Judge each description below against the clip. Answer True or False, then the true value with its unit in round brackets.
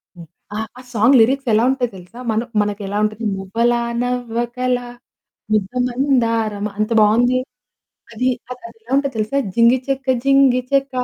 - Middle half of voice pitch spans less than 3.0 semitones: True (2.6 semitones)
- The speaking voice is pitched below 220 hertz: False (240 Hz)